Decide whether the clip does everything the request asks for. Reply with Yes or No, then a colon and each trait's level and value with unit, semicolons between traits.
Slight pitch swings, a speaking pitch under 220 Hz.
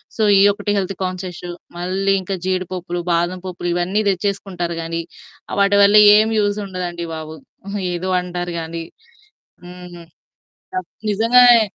Yes: narrow, 2.2 semitones; medium, 185 Hz